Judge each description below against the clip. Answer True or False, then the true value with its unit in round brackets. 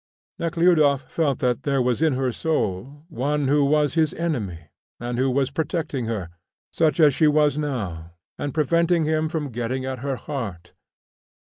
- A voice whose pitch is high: False (140 Hz)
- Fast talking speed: False (165 wpm)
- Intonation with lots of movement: False (3.8 semitones)